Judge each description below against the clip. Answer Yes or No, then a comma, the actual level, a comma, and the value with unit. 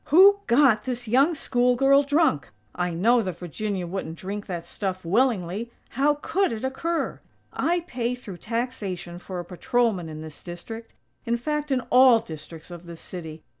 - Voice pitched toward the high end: Yes, high, 225 Hz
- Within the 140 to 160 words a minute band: No, average, 170 wpm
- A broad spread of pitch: Yes, wide, 6.8 semitones